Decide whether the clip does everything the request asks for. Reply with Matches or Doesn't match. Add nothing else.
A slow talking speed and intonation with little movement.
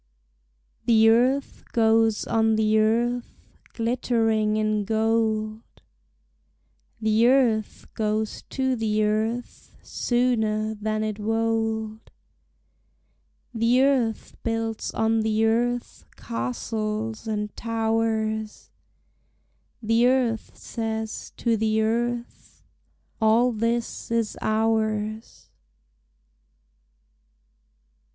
Matches